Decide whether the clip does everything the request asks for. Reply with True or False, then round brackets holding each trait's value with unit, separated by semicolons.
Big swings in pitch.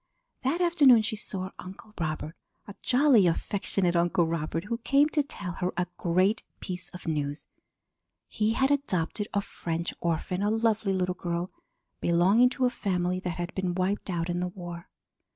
False (4.1 semitones)